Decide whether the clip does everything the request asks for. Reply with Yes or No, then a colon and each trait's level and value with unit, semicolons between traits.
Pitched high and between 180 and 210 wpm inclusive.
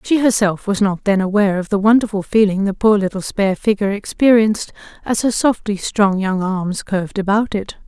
Yes: high, 205 Hz; average, 190 wpm